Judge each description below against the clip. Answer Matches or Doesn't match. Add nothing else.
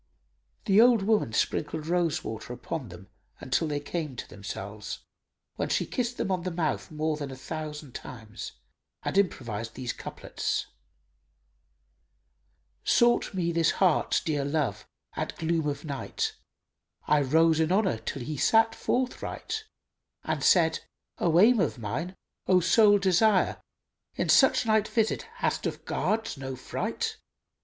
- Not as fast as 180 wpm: Matches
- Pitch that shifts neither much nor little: Doesn't match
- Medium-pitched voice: Matches